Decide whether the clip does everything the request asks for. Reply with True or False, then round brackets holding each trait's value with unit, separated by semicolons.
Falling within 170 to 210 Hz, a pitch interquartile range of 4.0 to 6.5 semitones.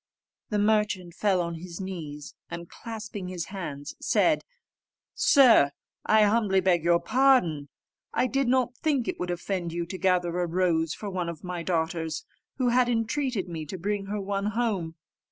True (185 Hz; 4.3 semitones)